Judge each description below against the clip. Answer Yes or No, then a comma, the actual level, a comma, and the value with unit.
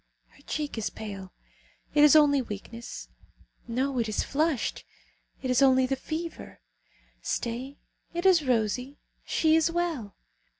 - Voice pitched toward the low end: No, very high, 265 Hz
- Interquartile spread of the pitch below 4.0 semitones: No, average, 4.8 semitones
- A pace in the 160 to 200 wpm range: No, slow, 135 wpm